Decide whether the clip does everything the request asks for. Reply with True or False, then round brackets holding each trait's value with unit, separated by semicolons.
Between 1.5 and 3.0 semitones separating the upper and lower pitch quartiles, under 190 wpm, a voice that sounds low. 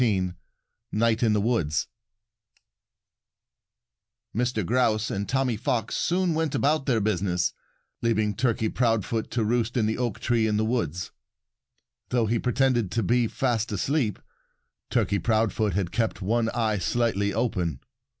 True (2.6 semitones; 140 wpm; 115 Hz)